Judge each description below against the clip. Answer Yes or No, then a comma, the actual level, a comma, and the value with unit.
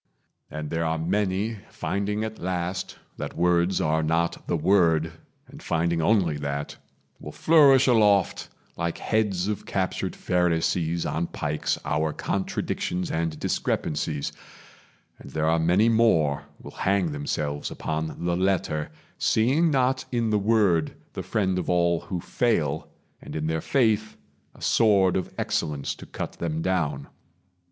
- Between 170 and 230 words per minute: No, average, 140 wpm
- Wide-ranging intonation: No, average, 4.5 semitones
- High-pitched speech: No, very low, 85 Hz